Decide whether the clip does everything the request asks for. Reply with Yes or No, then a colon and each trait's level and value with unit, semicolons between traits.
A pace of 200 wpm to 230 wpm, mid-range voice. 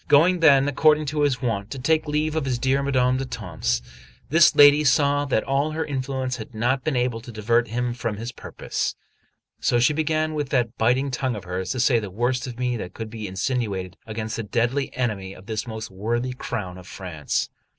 No: fast, 205 wpm; low, 125 Hz